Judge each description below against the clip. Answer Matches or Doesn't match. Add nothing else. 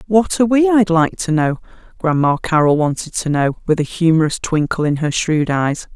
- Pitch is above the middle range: Doesn't match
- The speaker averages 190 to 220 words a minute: Matches